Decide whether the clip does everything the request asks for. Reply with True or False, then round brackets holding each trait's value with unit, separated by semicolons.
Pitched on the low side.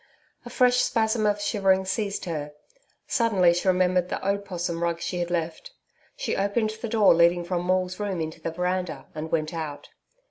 False (185 Hz)